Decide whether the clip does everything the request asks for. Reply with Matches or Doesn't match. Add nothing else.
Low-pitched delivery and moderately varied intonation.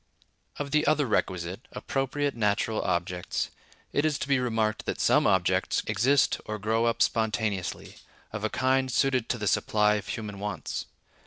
Matches